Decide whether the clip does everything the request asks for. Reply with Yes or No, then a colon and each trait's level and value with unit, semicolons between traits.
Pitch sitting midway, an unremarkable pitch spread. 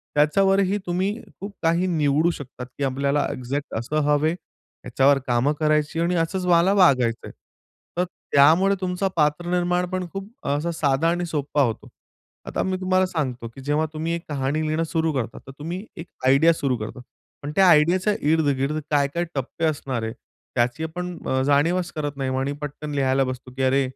Yes: medium, 150 Hz; average, 4.2 semitones